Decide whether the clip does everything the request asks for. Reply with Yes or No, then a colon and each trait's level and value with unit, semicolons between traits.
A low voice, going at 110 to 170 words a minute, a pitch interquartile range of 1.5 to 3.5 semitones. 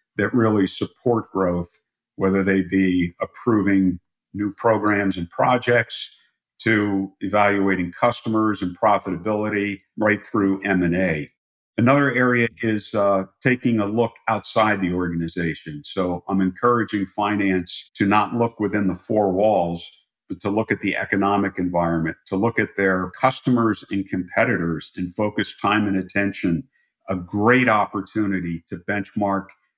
Yes: low, 100 Hz; slow, 135 wpm; narrow, 2.6 semitones